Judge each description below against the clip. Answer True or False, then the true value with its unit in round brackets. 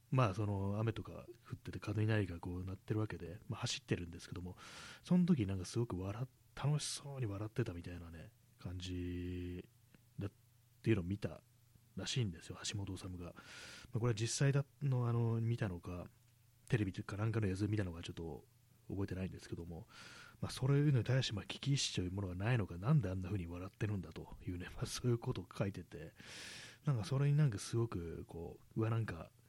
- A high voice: False (110 Hz)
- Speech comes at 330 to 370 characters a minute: False (400 characters per minute)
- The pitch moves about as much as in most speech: True (4.7 semitones)